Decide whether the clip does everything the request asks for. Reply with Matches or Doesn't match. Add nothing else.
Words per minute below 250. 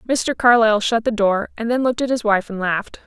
Doesn't match